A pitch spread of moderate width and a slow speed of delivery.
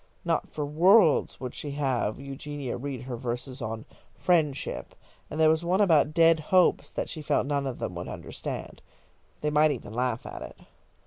No: average, 3.7 semitones; average, 180 wpm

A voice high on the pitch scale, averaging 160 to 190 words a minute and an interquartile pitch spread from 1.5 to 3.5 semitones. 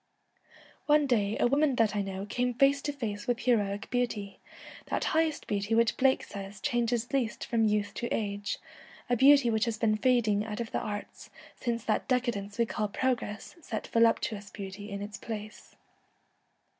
Yes: high, 225 Hz; average, 170 wpm; average, 3.1 semitones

